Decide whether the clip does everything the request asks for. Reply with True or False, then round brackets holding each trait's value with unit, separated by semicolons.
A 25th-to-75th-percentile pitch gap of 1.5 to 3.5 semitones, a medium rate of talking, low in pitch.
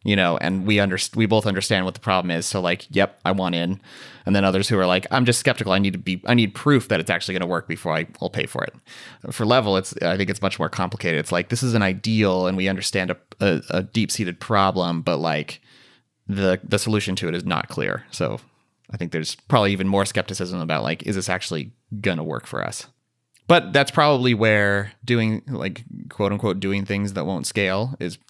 False (3.2 semitones; 235 wpm; 100 Hz)